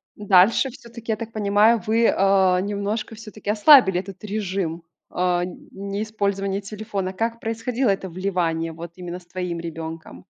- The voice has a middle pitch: No, high, 200 Hz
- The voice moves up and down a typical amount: Yes, average, 3.2 semitones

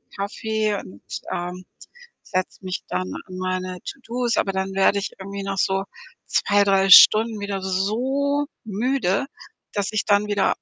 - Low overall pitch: No, high, 200 Hz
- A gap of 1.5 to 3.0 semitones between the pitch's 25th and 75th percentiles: Yes, narrow, 2.5 semitones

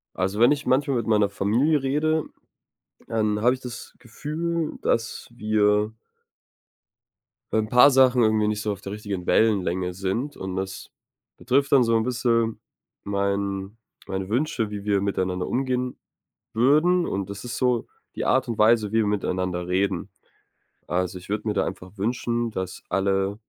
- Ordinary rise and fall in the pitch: Yes, average, 4.1 semitones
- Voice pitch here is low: Yes, low, 110 Hz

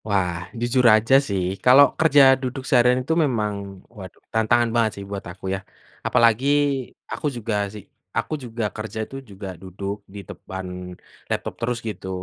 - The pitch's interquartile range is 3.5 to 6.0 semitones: Yes, average, 3.8 semitones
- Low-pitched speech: Yes, low, 110 Hz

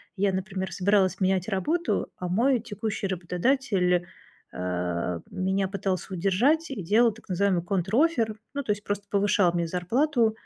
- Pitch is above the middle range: Yes, high, 195 Hz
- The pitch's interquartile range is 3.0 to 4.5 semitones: Yes, average, 3.5 semitones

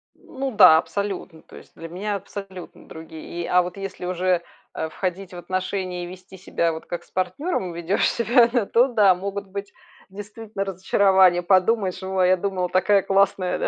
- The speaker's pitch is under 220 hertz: Yes, medium, 185 Hz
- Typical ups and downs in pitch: No, narrow, 1.9 semitones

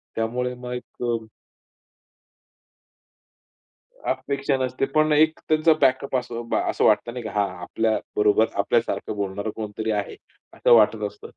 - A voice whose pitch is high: No, low, 120 Hz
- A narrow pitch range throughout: No, average, 3.2 semitones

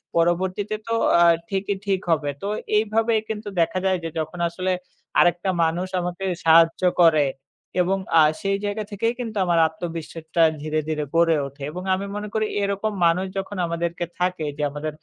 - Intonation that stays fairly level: No, average, 3.3 semitones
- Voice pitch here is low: No, medium, 180 Hz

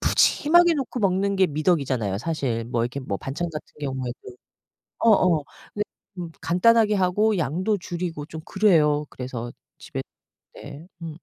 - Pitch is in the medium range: Yes, medium, 165 Hz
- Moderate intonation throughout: No, wide, 6.1 semitones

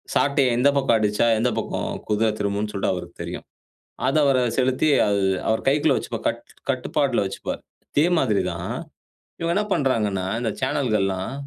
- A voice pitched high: No, low, 120 Hz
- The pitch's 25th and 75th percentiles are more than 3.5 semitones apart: Yes, average, 4.8 semitones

